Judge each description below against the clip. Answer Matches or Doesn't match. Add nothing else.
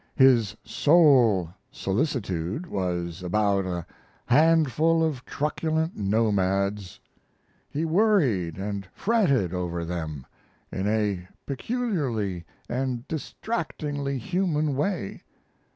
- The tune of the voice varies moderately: Doesn't match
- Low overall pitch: Matches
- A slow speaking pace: Matches